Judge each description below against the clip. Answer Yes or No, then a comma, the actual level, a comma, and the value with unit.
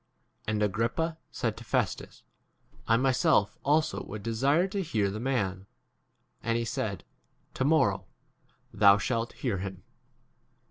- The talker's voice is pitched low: Yes, low, 115 Hz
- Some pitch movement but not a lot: Yes, average, 4.9 semitones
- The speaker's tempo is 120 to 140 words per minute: Yes, slow, 135 wpm